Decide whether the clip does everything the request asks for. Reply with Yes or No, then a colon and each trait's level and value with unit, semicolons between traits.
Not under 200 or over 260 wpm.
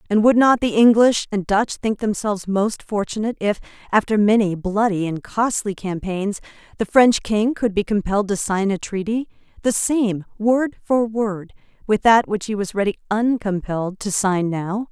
No: average, 175 wpm